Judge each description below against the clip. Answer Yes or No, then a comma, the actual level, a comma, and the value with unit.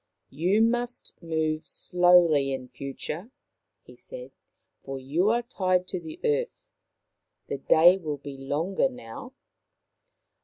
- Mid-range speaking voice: Yes, medium, 175 Hz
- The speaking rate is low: Yes, slow, 130 wpm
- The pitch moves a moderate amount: No, wide, 7.8 semitones